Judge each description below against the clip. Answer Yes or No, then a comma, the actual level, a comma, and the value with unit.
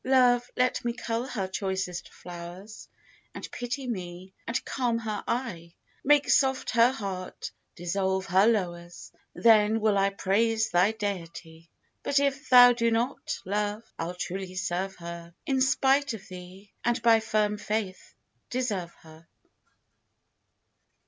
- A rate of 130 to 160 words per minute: Yes, slow, 135 wpm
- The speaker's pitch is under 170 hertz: No, high, 210 Hz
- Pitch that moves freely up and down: No, average, 4.6 semitones